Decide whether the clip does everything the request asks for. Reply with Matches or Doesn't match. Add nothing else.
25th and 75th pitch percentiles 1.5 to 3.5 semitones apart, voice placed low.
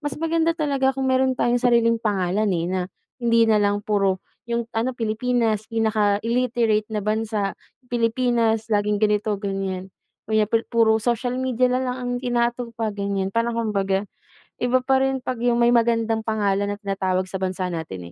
Doesn't match